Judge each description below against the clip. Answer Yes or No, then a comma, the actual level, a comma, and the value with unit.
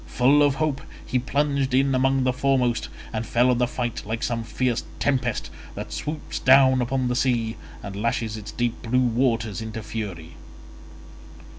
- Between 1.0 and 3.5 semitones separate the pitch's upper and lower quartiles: Yes, average, 2.7 semitones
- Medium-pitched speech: No, low, 125 Hz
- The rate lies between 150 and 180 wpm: Yes, average, 165 wpm